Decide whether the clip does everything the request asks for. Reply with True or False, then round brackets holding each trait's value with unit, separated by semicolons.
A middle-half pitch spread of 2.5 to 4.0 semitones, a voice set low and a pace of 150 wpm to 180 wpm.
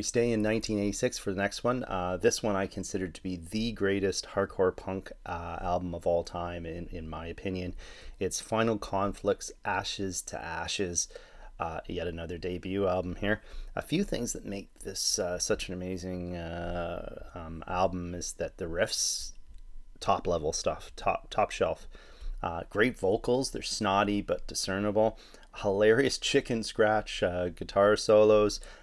True (3.1 semitones; 95 Hz; 155 wpm)